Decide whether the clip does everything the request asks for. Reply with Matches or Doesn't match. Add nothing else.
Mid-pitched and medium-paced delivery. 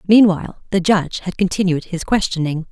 Matches